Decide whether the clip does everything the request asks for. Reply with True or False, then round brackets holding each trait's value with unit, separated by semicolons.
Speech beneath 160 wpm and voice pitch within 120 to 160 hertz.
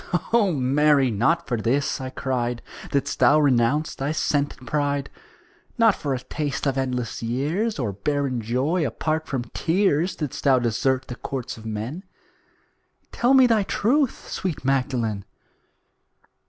True (145 wpm; 140 Hz)